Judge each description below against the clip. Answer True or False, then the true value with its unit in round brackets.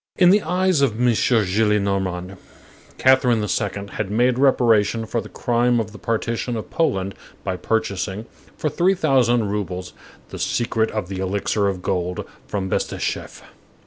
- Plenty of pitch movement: False (3.9 semitones)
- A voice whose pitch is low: True (110 Hz)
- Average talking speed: True (150 wpm)